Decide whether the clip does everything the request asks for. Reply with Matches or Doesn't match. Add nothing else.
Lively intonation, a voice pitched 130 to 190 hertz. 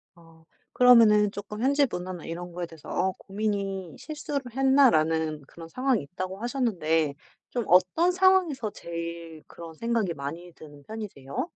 Matches